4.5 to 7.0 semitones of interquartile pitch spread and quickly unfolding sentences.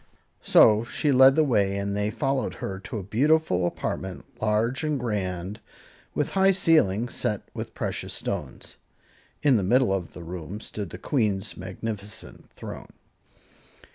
No: wide, 5.4 semitones; average, 145 wpm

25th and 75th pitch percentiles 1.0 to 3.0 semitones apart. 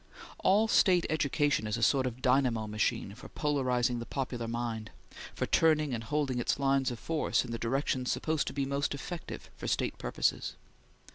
No: average, 3.8 semitones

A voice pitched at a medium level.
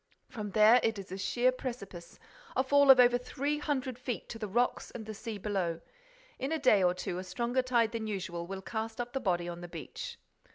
No: high, 225 Hz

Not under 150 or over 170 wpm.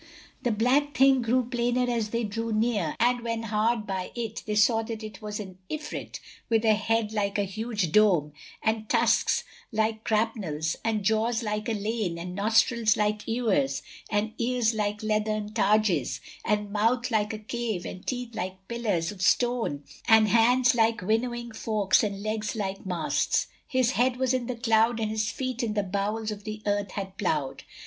No: average, 180 wpm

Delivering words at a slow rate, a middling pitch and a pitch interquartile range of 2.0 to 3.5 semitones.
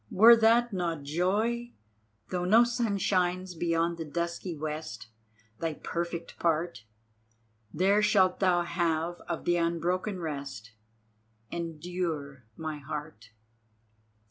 Yes: slow, 110 wpm; medium, 170 Hz; average, 2.8 semitones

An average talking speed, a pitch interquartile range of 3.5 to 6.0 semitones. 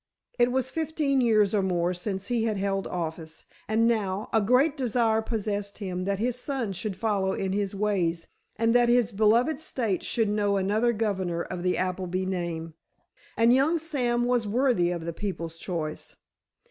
Yes: average, 170 wpm; average, 4.3 semitones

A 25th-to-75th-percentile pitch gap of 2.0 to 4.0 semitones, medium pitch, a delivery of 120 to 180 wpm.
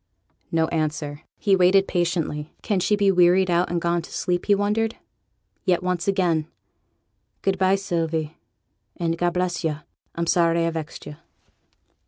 Yes: narrow, 2.4 semitones; medium, 175 Hz; average, 155 wpm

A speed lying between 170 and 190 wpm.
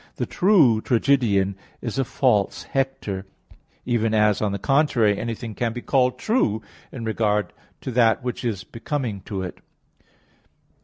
No: average, 155 wpm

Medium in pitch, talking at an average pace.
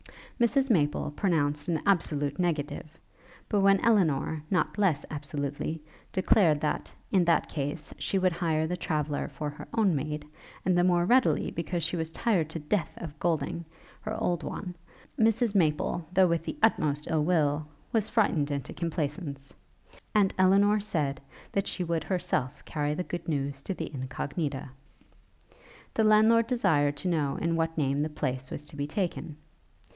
Yes: medium, 165 Hz; average, 160 wpm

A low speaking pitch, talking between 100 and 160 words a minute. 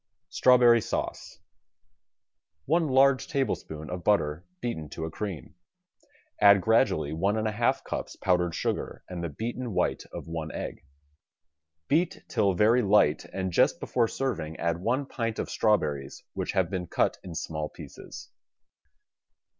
Yes: low, 100 Hz; average, 145 wpm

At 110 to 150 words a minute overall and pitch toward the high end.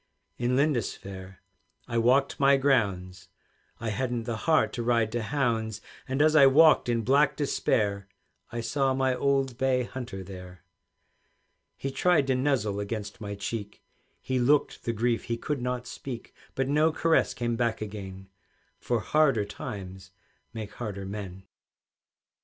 No: average, 145 wpm; low, 120 Hz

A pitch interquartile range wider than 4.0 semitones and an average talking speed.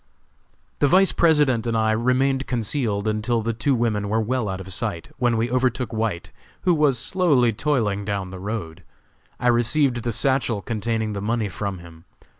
No: average, 3.7 semitones; average, 175 wpm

